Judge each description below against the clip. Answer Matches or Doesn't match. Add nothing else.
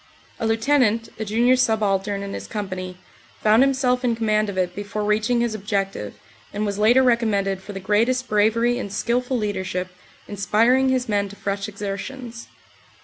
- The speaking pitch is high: Matches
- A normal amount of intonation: Matches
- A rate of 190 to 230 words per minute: Doesn't match